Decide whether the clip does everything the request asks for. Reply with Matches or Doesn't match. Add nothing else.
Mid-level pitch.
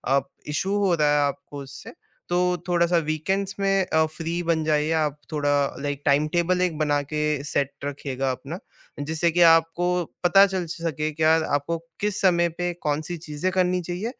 Matches